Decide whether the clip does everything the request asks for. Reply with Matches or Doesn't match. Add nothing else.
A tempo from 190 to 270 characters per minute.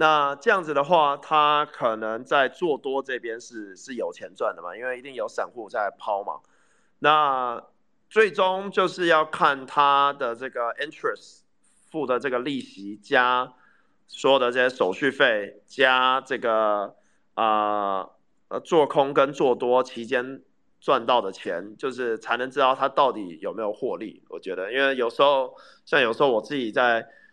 Matches